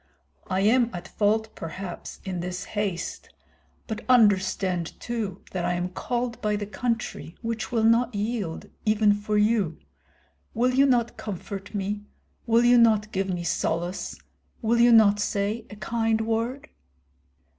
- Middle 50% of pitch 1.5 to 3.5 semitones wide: Yes, average, 3.2 semitones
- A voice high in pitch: Yes, high, 210 Hz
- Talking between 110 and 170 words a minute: Yes, average, 145 wpm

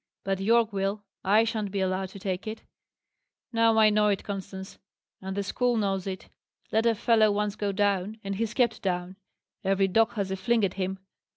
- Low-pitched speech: No, high, 200 Hz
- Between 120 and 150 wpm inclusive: No, average, 195 wpm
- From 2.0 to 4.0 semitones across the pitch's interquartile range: Yes, narrow, 2.4 semitones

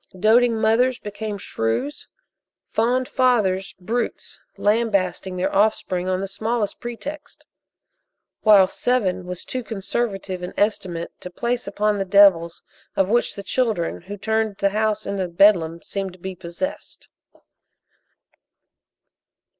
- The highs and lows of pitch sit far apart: No, average, 3.5 semitones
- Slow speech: Yes, slow, 120 wpm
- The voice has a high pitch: Yes, high, 200 Hz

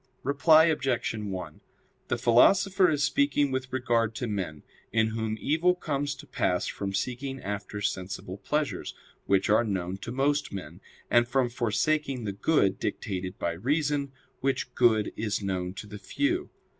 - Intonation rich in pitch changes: Yes, wide, 6.0 semitones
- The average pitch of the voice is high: No, low, 120 Hz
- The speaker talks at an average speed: Yes, average, 155 wpm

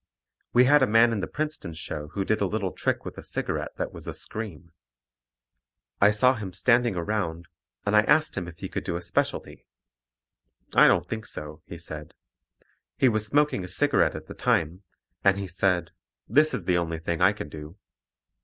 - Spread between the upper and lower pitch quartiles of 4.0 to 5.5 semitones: Yes, average, 4.9 semitones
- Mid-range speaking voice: No, low, 100 Hz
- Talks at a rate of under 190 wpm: No, average, 195 wpm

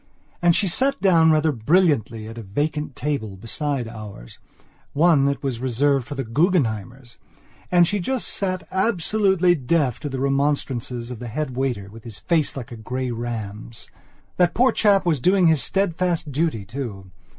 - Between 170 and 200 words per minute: No, average, 160 wpm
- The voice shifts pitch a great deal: Yes, wide, 6.5 semitones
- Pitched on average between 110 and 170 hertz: Yes, medium, 140 Hz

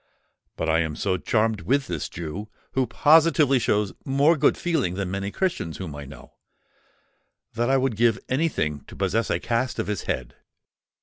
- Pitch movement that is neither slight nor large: No, wide, 7.1 semitones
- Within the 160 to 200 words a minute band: Yes, average, 180 wpm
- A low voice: Yes, low, 110 Hz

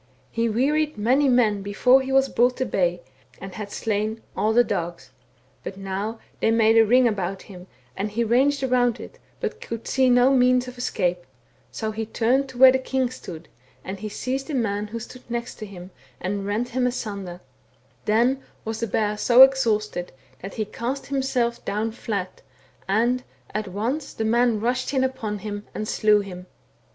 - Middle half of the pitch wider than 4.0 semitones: No, average, 3.7 semitones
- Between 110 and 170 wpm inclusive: No, average, 180 wpm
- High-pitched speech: Yes, high, 225 Hz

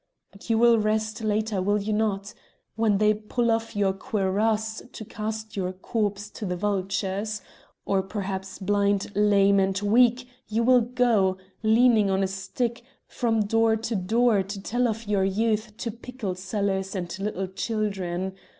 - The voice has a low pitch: No, high, 210 Hz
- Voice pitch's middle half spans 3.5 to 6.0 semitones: No, narrow, 2.5 semitones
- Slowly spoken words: No, average, 160 wpm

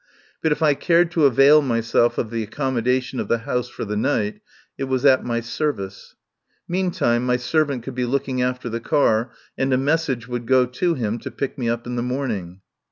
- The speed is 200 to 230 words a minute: Yes, fast, 205 wpm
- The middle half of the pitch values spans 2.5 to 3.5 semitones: Yes, average, 3.0 semitones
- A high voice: No, low, 125 Hz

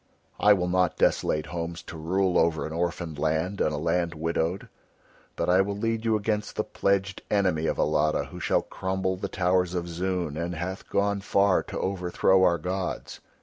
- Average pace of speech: Yes, average, 185 wpm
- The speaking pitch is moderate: No, very low, 90 Hz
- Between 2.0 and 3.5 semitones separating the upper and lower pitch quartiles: Yes, average, 2.7 semitones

